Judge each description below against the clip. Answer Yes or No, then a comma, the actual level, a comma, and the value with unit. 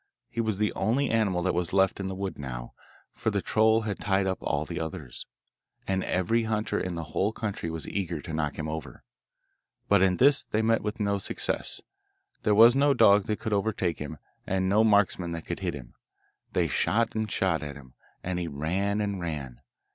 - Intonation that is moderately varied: Yes, average, 4.5 semitones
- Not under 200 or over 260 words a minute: Yes, fast, 205 wpm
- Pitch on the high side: No, very low, 95 Hz